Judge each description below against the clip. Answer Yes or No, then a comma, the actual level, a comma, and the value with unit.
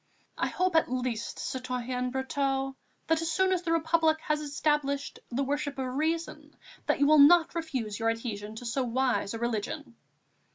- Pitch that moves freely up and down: No, average, 4.2 semitones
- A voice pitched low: No, very high, 275 Hz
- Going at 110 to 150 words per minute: No, average, 165 wpm